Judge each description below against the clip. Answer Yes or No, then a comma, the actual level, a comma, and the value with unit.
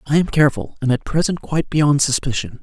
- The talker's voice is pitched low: No, medium, 145 Hz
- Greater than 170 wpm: Yes, fast, 205 wpm